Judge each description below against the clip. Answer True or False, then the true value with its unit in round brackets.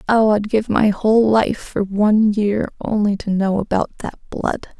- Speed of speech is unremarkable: True (190 wpm)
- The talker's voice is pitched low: False (210 Hz)